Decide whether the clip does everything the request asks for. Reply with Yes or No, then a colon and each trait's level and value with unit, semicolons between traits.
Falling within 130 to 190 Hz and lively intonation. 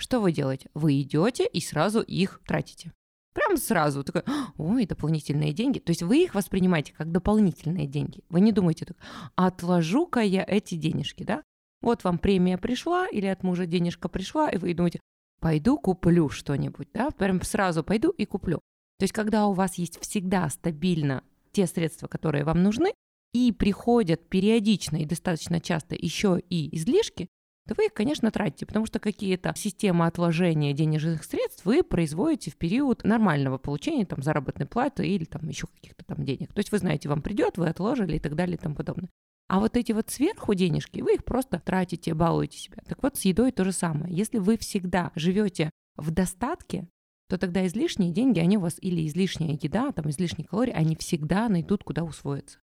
No: medium, 185 Hz; average, 4.5 semitones